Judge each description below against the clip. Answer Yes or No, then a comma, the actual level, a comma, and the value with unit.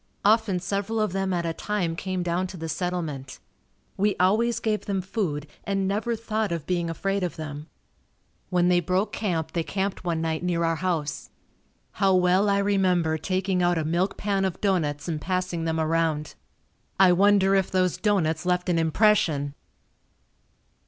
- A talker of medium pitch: Yes, medium, 180 Hz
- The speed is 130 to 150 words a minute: No, average, 170 wpm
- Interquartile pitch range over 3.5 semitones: No, average, 3.0 semitones